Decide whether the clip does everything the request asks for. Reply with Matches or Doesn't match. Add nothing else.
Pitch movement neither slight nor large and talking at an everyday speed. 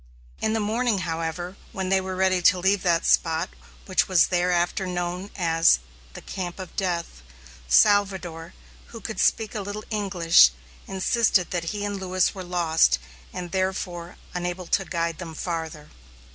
Doesn't match